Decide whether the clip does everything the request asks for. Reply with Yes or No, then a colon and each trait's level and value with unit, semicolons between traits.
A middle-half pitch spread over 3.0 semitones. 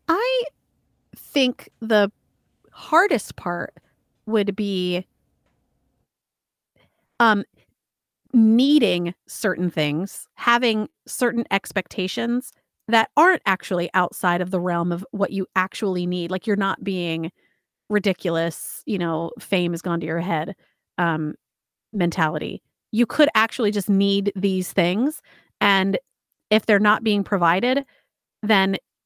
Yes: average, 4.0 semitones